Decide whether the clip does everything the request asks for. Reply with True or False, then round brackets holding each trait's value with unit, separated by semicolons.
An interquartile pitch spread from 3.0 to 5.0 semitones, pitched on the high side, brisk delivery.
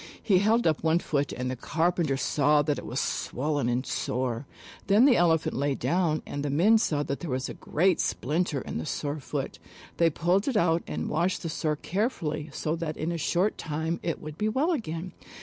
False (3.6 semitones; 160 Hz; 210 wpm)